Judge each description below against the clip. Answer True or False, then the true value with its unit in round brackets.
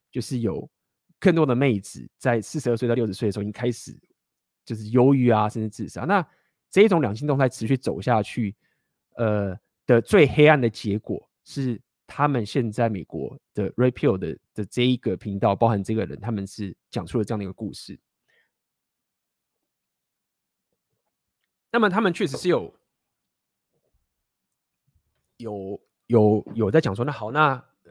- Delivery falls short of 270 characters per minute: True (240 characters per minute)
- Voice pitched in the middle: False (115 Hz)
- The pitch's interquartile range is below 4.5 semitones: True (3.8 semitones)